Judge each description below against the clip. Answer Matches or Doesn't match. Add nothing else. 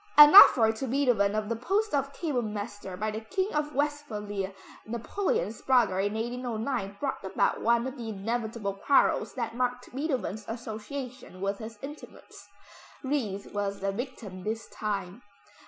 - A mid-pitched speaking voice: Doesn't match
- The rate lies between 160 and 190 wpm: Doesn't match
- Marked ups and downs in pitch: Doesn't match